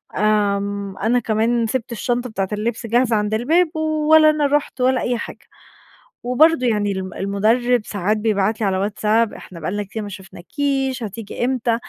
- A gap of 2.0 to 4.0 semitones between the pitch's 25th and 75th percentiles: Yes, average, 3.5 semitones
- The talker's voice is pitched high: Yes, high, 225 Hz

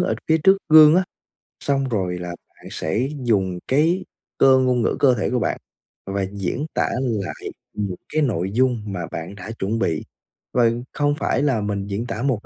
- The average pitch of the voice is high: No, low, 115 Hz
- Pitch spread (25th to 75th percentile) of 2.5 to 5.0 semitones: No, wide, 5.6 semitones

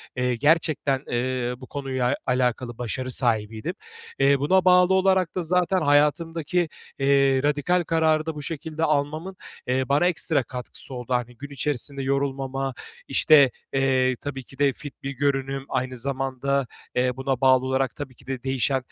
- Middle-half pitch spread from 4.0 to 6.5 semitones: No, average, 2.7 semitones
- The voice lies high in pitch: No, low, 135 Hz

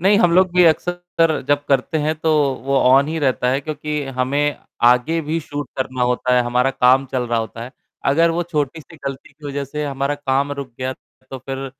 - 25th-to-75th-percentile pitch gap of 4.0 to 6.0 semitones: No, average, 3.3 semitones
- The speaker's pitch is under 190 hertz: Yes, medium, 140 Hz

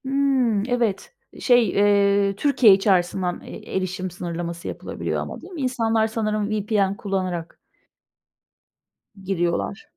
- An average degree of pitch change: Yes, average, 3.9 semitones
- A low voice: No, high, 200 Hz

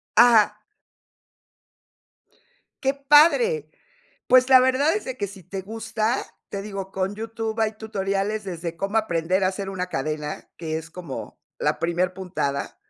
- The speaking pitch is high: Yes, high, 200 Hz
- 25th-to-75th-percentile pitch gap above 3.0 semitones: Yes, average, 3.9 semitones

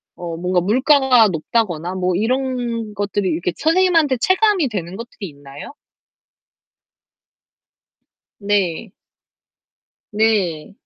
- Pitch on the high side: Yes, high, 205 Hz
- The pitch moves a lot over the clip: Yes, wide, 6.1 semitones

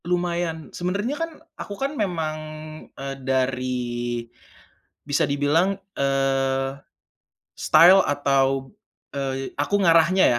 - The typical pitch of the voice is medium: Yes, medium, 145 Hz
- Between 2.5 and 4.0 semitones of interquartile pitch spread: No, average, 4.7 semitones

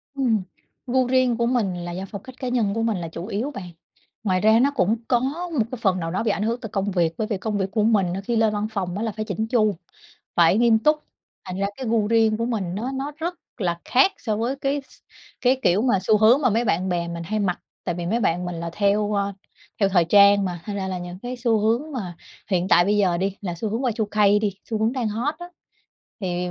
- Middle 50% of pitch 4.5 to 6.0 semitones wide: No, average, 3.9 semitones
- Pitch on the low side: No, high, 210 Hz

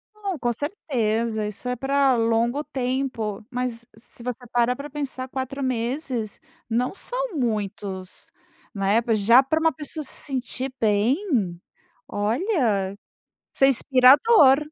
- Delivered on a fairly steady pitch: No, average, 3.7 semitones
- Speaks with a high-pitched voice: Yes, very high, 250 Hz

